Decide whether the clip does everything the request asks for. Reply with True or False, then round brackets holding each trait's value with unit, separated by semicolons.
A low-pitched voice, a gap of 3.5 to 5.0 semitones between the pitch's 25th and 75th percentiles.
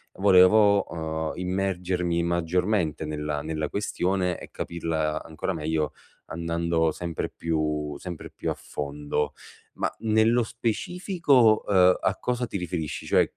True (85 Hz; 3.9 semitones)